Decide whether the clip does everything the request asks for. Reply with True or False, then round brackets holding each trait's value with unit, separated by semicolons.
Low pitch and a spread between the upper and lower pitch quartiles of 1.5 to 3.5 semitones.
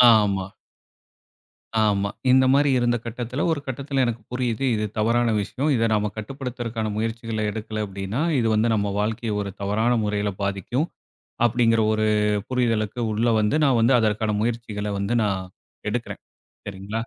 True (110 Hz; 2.5 semitones)